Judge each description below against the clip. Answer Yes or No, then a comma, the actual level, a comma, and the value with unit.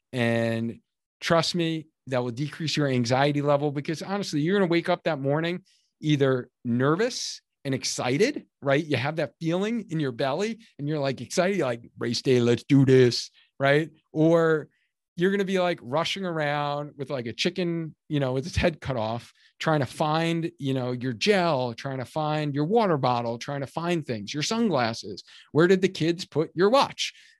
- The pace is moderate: Yes, average, 190 wpm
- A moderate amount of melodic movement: Yes, average, 4.3 semitones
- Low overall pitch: No, medium, 150 Hz